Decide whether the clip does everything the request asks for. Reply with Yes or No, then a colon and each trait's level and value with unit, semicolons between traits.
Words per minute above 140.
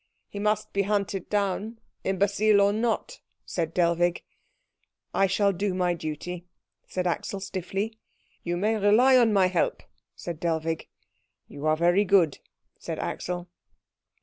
No: slow, 135 wpm